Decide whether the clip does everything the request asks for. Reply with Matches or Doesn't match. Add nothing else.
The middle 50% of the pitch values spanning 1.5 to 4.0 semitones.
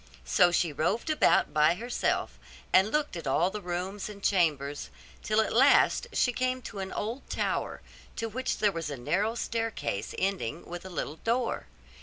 Doesn't match